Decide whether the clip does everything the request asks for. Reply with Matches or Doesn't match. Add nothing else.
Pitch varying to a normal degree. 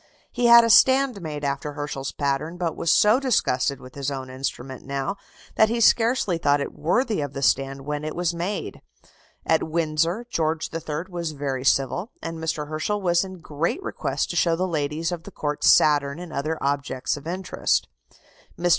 Matches